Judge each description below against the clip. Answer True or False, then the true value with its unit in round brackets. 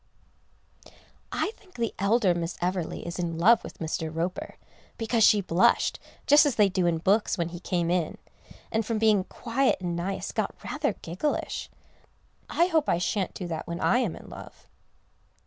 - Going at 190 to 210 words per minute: False (175 wpm)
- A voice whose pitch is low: False (190 Hz)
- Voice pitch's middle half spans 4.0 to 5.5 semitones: True (5.0 semitones)